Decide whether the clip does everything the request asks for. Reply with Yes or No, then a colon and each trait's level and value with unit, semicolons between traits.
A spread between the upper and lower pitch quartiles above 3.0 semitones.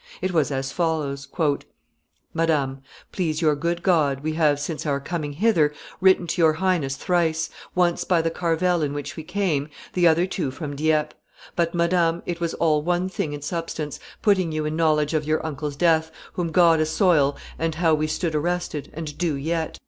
No: narrow, 2.5 semitones